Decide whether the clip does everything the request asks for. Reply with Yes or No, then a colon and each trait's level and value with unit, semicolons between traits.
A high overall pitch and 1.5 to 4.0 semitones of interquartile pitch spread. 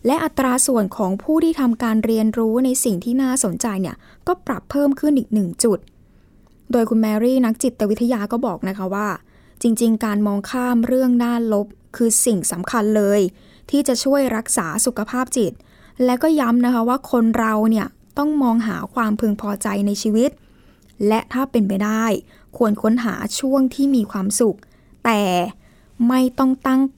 Yes: high, 230 Hz; average, 3.4 semitones